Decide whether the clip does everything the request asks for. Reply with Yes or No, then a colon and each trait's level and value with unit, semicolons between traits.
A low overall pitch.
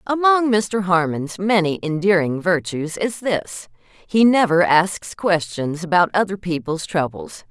No: medium, 185 Hz